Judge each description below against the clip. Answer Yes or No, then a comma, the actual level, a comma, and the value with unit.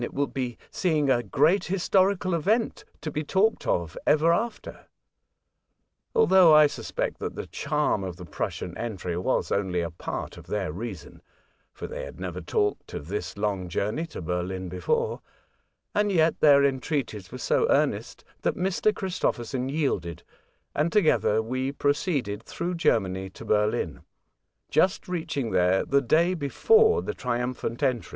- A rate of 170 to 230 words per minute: No, average, 150 wpm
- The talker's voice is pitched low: Yes, low, 130 Hz